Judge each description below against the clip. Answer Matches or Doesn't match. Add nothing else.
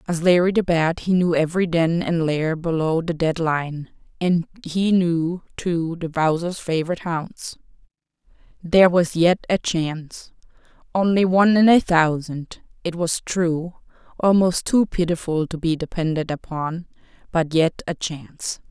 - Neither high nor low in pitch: Matches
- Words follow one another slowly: Doesn't match